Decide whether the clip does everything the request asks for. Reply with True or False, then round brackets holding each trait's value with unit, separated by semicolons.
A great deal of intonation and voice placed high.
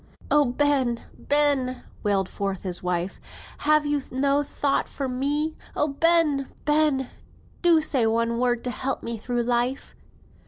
False (3.6 semitones; 265 Hz)